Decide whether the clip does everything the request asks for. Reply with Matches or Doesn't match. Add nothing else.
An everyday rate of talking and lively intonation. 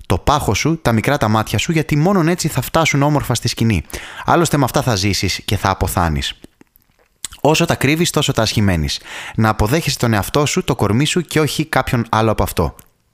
Doesn't match